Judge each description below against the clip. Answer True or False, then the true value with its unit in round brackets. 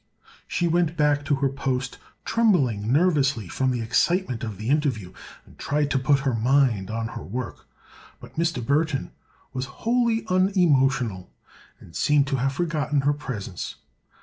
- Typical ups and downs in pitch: True (4.1 semitones)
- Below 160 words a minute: True (150 wpm)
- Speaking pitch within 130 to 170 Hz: True (140 Hz)